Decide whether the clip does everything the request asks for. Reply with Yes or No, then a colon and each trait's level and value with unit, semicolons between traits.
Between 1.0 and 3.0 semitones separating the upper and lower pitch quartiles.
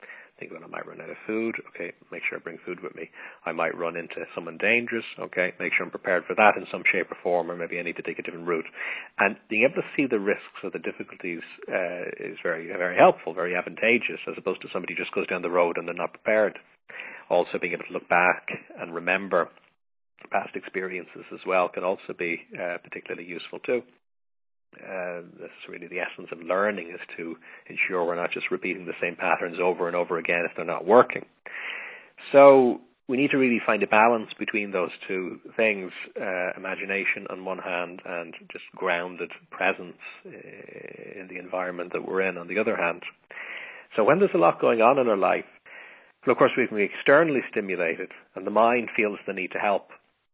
No: average, 4.7 semitones